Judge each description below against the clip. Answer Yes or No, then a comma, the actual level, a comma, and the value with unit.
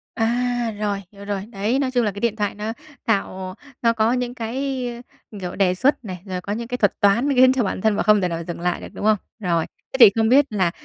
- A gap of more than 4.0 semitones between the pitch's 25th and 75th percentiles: No, average, 3.7 semitones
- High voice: Yes, high, 215 Hz